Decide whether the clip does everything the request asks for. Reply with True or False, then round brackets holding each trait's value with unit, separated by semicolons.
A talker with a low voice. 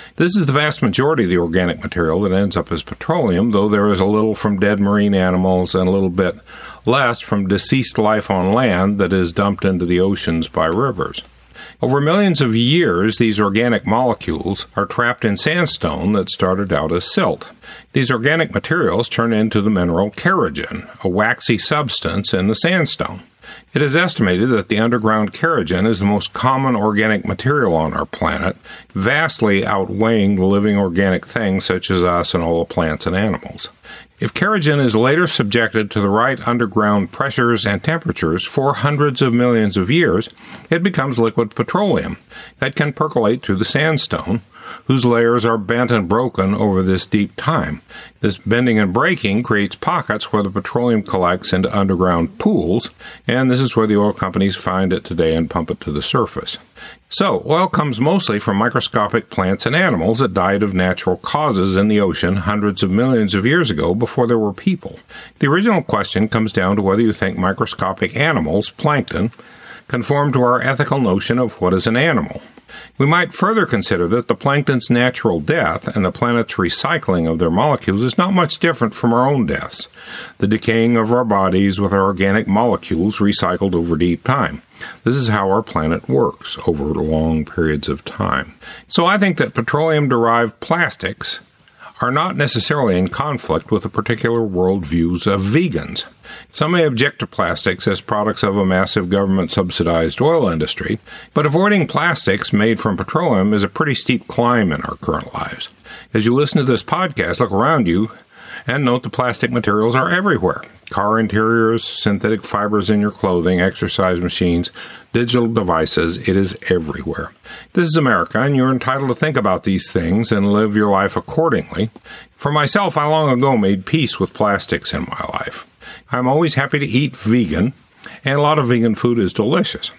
True (110 Hz)